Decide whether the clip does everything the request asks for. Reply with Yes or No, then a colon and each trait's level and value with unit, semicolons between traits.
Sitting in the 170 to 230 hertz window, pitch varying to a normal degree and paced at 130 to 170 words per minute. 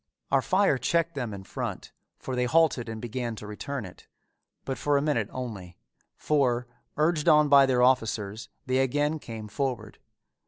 No: low, 130 Hz; average, 4.4 semitones; average, 165 wpm